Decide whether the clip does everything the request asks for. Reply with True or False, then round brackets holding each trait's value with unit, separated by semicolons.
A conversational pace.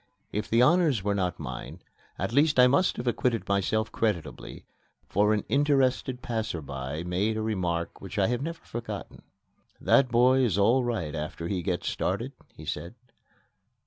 True (165 wpm)